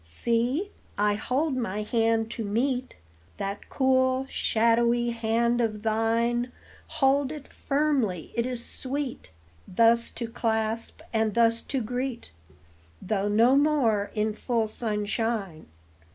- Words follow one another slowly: Yes, slow, 120 wpm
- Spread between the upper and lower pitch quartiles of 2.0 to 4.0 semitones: Yes, average, 2.7 semitones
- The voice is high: Yes, high, 230 Hz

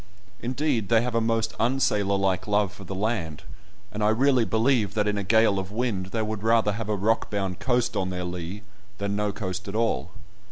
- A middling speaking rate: No, fast, 210 wpm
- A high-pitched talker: No, low, 105 Hz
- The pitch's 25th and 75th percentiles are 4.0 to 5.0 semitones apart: No, average, 2.8 semitones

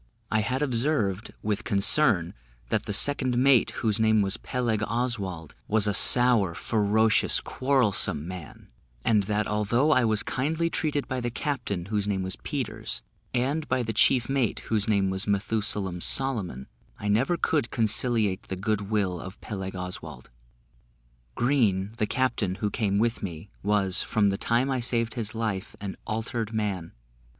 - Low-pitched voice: Yes, low, 110 Hz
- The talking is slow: No, average, 160 wpm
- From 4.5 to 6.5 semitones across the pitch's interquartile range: No, average, 3.7 semitones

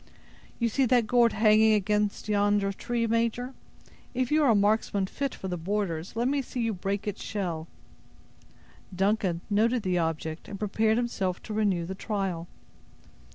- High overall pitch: Yes, high, 210 Hz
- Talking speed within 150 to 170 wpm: Yes, average, 160 wpm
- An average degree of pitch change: Yes, average, 3.3 semitones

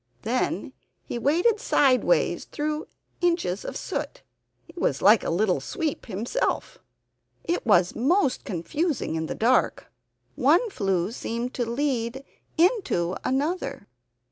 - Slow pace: Yes, slow, 120 wpm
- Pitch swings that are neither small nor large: No, wide, 8.2 semitones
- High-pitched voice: Yes, very high, 255 Hz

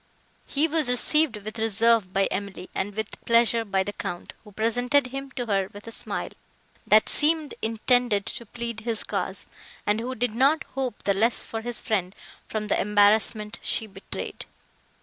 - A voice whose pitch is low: No, high, 225 Hz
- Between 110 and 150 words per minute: No, average, 170 wpm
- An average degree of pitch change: Yes, average, 3.1 semitones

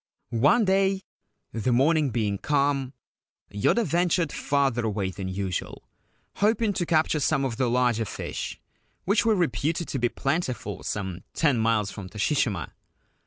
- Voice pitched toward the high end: No, low, 135 Hz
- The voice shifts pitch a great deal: Yes, wide, 7.1 semitones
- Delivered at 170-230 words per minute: No, average, 140 wpm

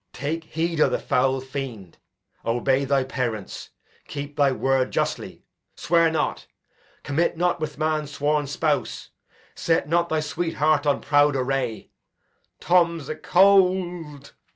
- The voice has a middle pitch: Yes, medium, 145 Hz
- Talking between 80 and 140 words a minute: Yes, slow, 135 wpm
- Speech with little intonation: No, average, 3.5 semitones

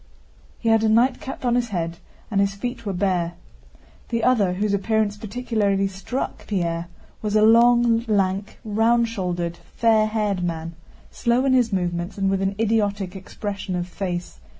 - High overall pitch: Yes, high, 205 Hz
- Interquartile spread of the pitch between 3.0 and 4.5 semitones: Yes, average, 3.4 semitones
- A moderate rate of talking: Yes, average, 160 wpm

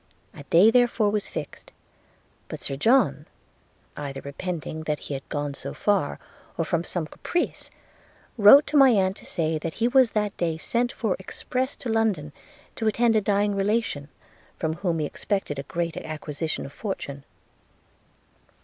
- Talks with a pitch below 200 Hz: Yes, medium, 185 Hz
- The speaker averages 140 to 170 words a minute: Yes, average, 160 wpm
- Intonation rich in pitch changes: Yes, wide, 6.4 semitones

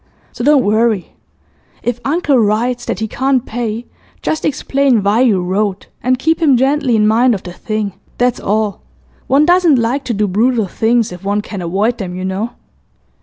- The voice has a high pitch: Yes, high, 230 Hz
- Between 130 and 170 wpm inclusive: No, average, 180 wpm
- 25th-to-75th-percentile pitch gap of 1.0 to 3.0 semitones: No, average, 3.9 semitones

